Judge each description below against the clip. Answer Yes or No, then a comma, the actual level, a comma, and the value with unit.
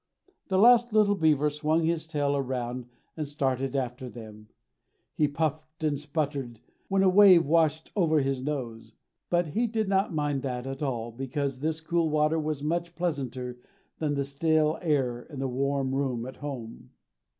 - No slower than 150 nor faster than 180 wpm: Yes, average, 165 wpm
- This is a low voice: No, medium, 145 Hz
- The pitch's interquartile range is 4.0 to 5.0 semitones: No, average, 3.4 semitones